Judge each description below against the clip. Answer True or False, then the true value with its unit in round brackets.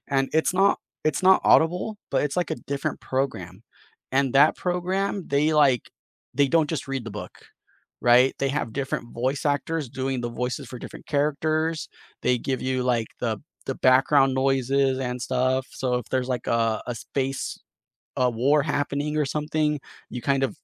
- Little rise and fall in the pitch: False (3.0 semitones)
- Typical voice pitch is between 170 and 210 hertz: False (135 Hz)